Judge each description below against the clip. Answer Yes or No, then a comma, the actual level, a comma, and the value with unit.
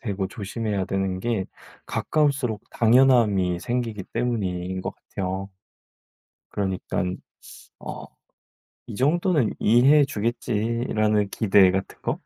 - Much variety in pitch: No, average, 4.1 semitones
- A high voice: No, low, 105 Hz